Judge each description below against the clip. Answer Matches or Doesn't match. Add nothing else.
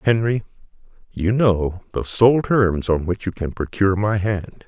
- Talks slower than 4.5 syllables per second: Matches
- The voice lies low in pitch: Matches